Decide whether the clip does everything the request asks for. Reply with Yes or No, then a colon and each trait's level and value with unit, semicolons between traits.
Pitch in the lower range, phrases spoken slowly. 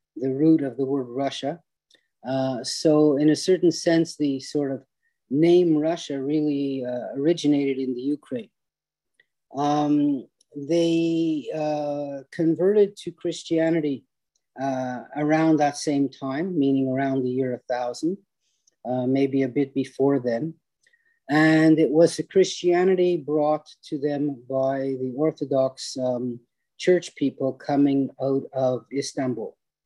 No: medium, 145 Hz; slow, 125 wpm